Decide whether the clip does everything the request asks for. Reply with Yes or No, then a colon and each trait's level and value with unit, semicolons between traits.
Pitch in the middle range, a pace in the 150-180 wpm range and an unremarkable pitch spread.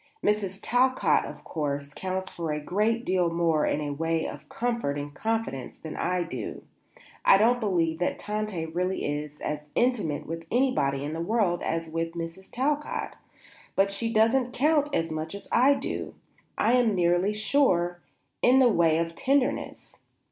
No: medium, 180 Hz; average, 165 wpm; wide, 6.0 semitones